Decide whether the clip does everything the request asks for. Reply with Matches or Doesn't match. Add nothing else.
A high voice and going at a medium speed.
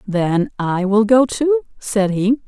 Matches